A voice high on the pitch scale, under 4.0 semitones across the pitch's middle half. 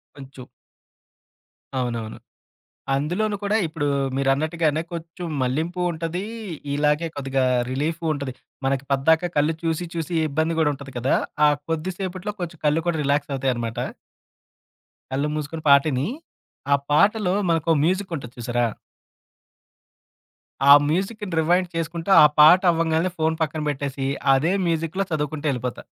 No: medium, 155 Hz; average, 3.5 semitones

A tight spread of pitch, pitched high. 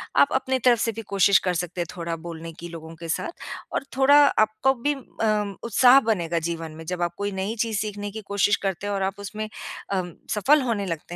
No: average, 4.6 semitones; high, 200 Hz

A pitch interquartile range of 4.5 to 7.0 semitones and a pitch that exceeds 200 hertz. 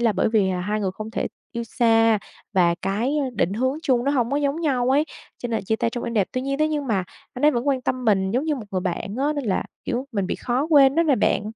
Yes: average, 4.8 semitones; high, 240 Hz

